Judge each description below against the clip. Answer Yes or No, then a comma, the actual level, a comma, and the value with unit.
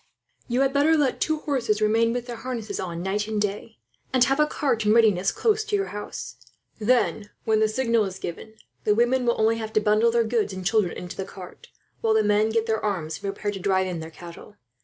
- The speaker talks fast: Yes, fast, 230 wpm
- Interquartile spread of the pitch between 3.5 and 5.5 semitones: No, average, 2.9 semitones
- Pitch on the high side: Yes, high, 220 Hz